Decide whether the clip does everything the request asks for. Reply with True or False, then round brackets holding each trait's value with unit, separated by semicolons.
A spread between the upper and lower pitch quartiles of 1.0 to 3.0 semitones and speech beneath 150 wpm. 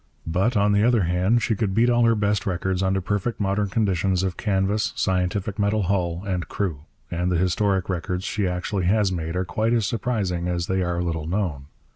False (2.7 semitones; 200 wpm)